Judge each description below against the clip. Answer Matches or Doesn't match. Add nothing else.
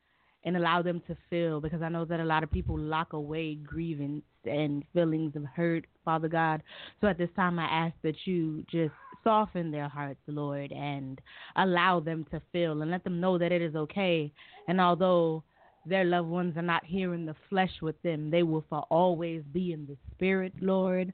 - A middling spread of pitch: Doesn't match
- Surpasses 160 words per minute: Matches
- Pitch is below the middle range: Doesn't match